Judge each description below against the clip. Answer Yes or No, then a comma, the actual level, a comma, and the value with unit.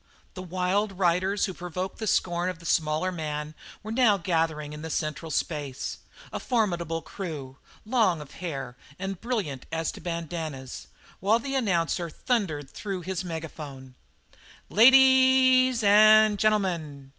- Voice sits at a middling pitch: Yes, medium, 180 Hz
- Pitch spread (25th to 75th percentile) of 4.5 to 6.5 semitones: Yes, average, 5.1 semitones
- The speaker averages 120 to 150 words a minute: Yes, average, 145 wpm